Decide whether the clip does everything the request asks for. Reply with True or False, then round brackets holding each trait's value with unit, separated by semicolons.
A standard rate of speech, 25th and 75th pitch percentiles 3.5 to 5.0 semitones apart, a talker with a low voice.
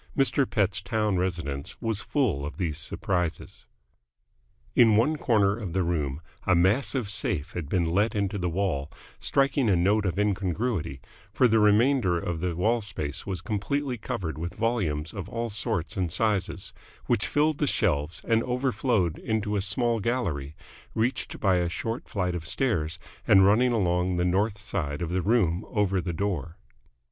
True (165 wpm; 4.6 semitones; 100 Hz)